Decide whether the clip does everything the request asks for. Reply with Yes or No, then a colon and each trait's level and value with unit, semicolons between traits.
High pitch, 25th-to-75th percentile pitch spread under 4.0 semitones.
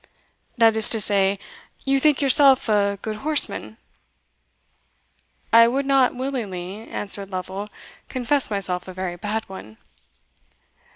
No: high, 215 Hz; average, 5.1 semitones